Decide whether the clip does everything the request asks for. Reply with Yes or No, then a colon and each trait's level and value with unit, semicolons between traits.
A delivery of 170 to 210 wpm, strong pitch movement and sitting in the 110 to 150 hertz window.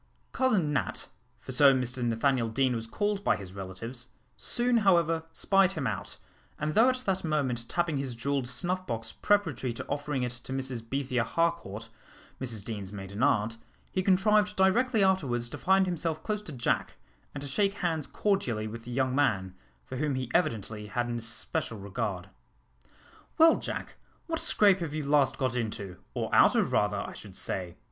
Yes: average, 175 wpm; wide, 7.9 semitones; low, 135 Hz